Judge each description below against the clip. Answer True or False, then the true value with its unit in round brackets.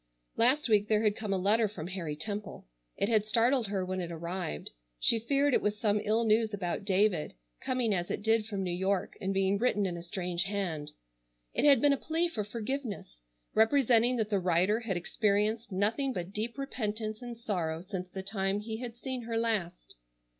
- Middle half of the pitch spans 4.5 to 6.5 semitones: False (3.4 semitones)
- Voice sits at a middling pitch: False (210 Hz)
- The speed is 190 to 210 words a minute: True (195 wpm)